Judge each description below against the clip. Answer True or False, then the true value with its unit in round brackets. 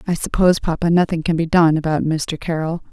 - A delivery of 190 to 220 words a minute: True (205 wpm)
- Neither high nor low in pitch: True (165 Hz)